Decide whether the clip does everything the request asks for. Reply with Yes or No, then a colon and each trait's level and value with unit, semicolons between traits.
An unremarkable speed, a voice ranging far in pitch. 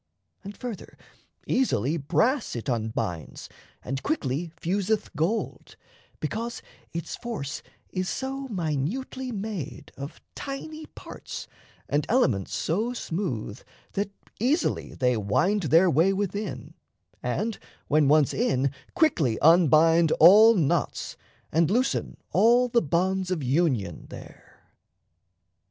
No: slow, 110 wpm; wide, 7.8 semitones